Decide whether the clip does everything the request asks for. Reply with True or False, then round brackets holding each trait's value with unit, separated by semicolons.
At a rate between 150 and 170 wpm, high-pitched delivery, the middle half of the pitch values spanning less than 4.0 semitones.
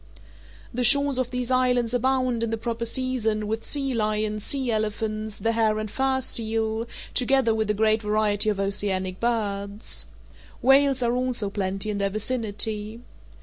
True (155 wpm; 225 Hz; 2.9 semitones)